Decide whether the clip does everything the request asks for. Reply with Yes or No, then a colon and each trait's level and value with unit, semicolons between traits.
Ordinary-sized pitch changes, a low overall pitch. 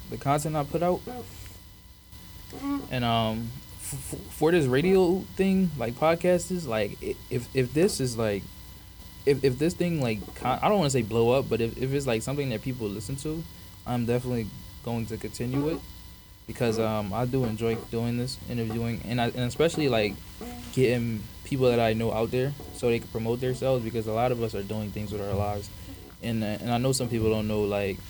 Yes: average, 4.0 semitones; low, 115 Hz